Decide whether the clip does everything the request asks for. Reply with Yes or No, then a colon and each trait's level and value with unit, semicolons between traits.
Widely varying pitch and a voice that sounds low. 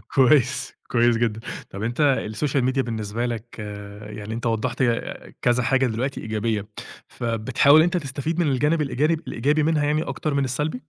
No: average, 4.2 semitones; low, 130 Hz